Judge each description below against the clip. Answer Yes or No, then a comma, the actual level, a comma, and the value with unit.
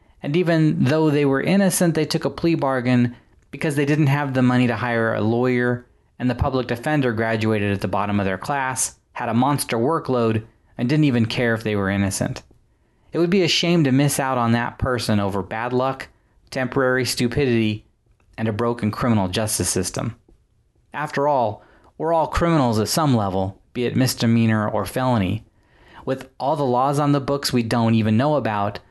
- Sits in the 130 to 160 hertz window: No, low, 120 Hz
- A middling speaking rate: Yes, average, 190 wpm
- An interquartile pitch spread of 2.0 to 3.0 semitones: No, average, 4.2 semitones